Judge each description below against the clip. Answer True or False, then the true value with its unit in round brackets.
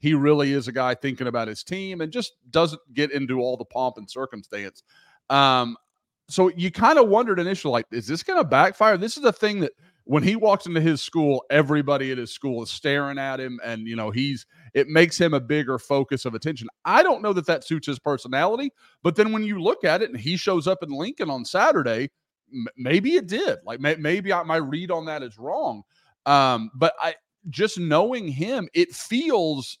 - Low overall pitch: False (150 Hz)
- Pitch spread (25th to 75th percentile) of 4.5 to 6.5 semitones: True (5.5 semitones)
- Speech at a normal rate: False (210 wpm)